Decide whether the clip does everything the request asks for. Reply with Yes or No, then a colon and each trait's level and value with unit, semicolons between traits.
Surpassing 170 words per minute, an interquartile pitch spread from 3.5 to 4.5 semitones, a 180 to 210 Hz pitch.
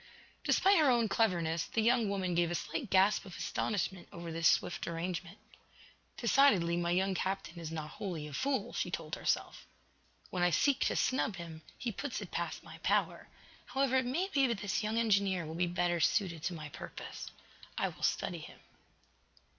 No: average, 185 wpm; average, 5.2 semitones; high, 190 Hz